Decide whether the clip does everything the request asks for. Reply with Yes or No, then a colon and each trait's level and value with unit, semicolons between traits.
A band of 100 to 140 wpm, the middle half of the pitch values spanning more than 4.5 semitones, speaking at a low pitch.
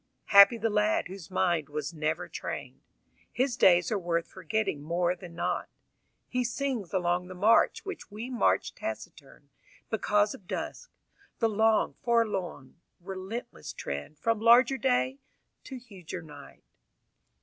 No: slow, 135 wpm; average, 4.9 semitones; high, 200 Hz